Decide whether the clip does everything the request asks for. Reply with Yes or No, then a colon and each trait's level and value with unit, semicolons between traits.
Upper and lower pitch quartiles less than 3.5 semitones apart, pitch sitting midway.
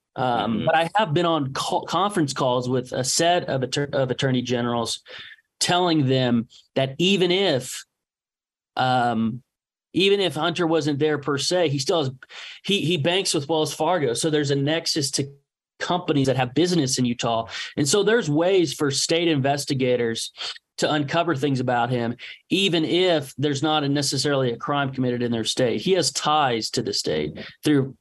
No: average, 4.5 semitones; medium, 145 Hz